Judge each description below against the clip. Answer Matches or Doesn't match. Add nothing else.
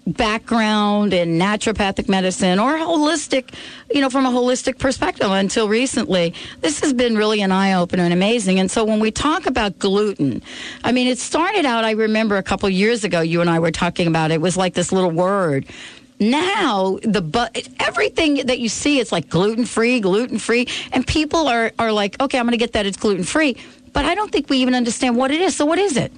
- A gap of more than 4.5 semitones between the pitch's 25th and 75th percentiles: Matches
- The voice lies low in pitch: Doesn't match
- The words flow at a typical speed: Doesn't match